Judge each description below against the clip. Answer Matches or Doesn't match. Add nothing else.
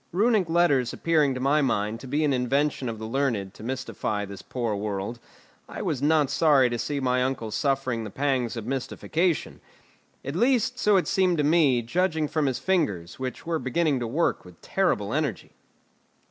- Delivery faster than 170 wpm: Matches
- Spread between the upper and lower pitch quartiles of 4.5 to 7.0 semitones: Matches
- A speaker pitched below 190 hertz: Matches